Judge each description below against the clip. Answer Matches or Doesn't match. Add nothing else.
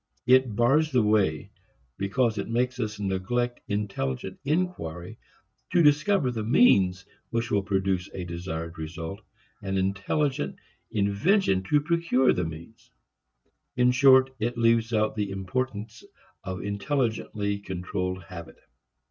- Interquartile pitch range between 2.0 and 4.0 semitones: Doesn't match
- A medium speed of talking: Doesn't match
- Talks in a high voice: Doesn't match